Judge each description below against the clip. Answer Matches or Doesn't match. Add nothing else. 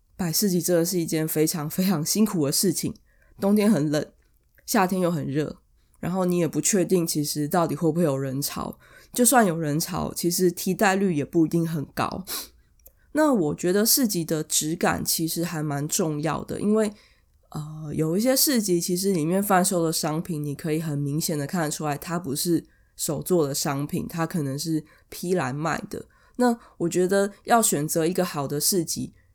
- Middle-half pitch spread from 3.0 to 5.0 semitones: Matches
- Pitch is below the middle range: Doesn't match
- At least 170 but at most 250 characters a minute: Doesn't match